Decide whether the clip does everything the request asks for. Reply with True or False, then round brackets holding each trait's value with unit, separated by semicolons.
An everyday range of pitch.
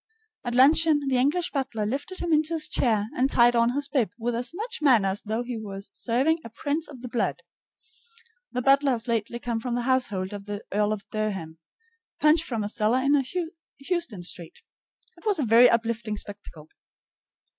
True (4.7 semitones)